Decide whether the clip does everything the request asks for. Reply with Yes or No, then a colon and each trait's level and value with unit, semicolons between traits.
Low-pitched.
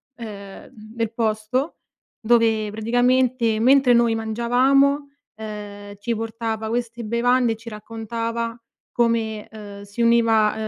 No: high, 230 Hz